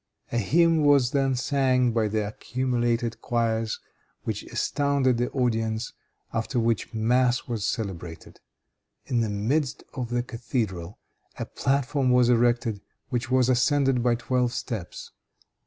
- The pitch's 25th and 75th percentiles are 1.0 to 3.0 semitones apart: Yes, narrow, 2.4 semitones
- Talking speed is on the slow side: Yes, slow, 130 wpm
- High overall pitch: No, low, 120 Hz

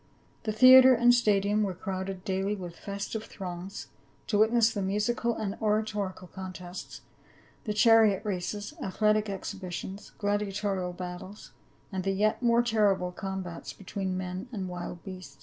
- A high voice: Yes, high, 200 Hz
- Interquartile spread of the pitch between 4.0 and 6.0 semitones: No, narrow, 2.4 semitones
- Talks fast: No, slow, 135 wpm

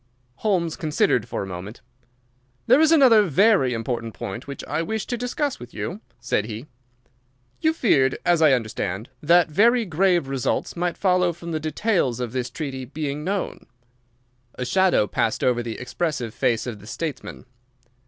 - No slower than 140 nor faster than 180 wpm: Yes, average, 165 wpm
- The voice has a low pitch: No, medium, 150 Hz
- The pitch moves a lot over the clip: Yes, wide, 7.5 semitones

